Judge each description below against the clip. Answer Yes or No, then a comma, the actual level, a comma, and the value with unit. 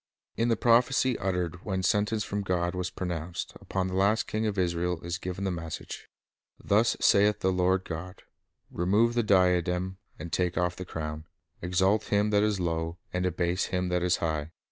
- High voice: No, very low, 90 Hz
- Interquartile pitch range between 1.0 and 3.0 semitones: Yes, narrow, 2.6 semitones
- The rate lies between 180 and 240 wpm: Yes, average, 185 wpm